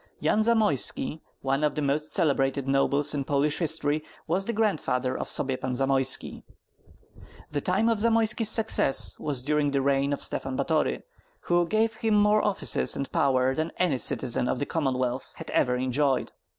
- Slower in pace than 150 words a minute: No, average, 165 wpm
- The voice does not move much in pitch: No, average, 5.2 semitones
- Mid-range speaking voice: Yes, medium, 145 Hz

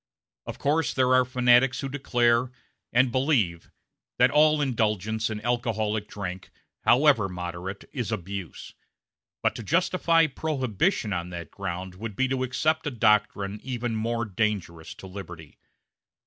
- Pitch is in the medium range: No, low, 115 Hz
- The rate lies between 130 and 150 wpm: Yes, average, 140 wpm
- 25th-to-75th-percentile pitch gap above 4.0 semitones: Yes, average, 4.7 semitones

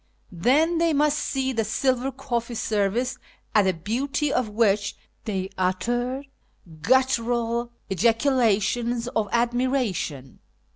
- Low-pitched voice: No, high, 235 Hz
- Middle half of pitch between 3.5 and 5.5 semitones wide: Yes, average, 3.9 semitones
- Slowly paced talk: Yes, slow, 110 wpm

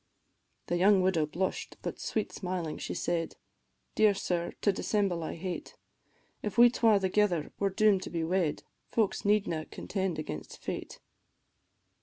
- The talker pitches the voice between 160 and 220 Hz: Yes, medium, 185 Hz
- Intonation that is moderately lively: Yes, average, 3.3 semitones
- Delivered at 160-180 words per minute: No, average, 145 wpm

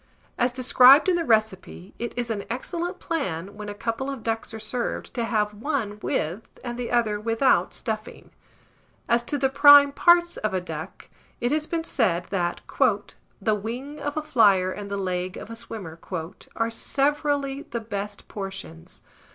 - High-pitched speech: Yes, high, 230 Hz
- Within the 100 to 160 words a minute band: No, average, 170 wpm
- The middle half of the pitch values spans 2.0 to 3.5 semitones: No, average, 5.2 semitones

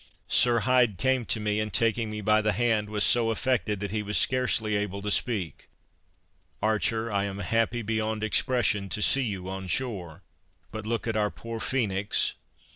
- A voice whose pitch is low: Yes, low, 110 Hz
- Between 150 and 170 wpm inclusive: No, average, 180 wpm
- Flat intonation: Yes, narrow, 2.1 semitones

